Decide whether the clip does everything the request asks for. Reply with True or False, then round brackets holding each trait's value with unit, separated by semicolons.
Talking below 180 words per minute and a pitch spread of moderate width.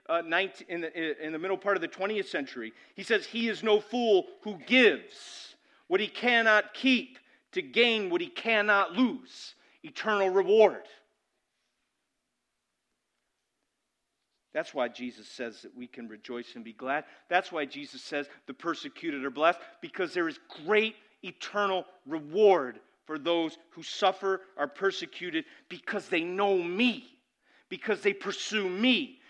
False (145 wpm; 6.5 semitones)